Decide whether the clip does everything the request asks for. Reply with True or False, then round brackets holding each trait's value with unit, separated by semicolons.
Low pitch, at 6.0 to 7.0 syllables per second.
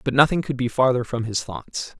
False (125 Hz; 5.3 syllables/s)